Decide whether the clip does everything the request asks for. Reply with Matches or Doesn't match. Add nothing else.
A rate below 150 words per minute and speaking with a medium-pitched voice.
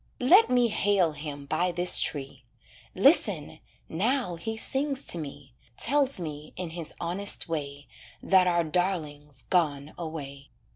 Matches